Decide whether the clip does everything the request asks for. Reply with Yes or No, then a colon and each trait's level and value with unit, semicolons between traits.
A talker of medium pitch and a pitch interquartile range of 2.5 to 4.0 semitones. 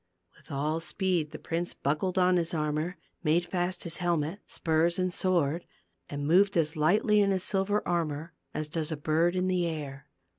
Yes: medium, 170 Hz; average, 3.0 semitones